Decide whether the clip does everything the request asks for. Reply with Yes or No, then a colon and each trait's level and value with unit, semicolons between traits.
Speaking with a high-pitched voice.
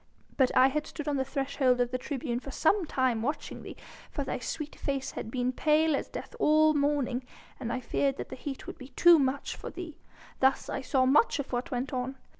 Yes: very high, 270 Hz